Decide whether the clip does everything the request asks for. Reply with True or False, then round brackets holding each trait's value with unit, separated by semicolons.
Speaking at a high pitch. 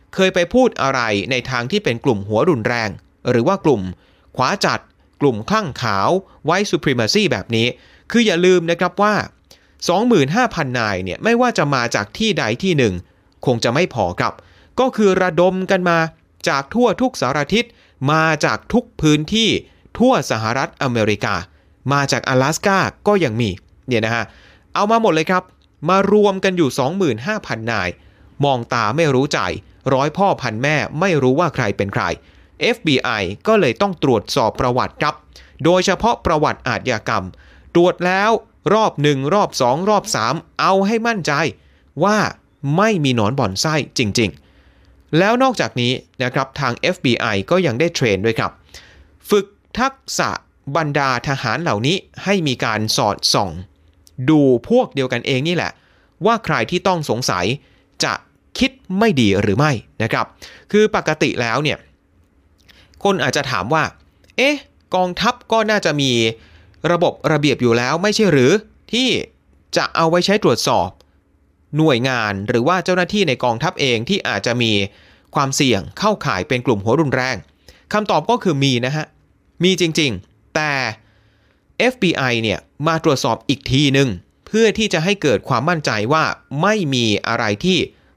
False (140 Hz)